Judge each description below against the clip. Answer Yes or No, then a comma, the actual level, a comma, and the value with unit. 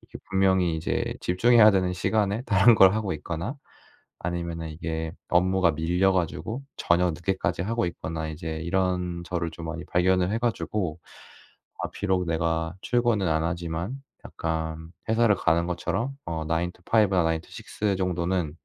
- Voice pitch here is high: No, very low, 90 Hz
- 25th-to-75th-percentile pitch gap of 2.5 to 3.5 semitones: Yes, average, 2.9 semitones